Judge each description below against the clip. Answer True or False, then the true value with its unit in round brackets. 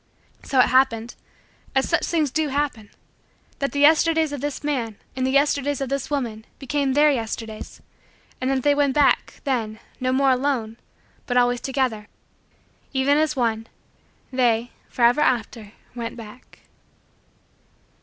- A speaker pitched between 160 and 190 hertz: False (260 Hz)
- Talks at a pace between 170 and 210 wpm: False (145 wpm)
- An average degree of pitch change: True (3.5 semitones)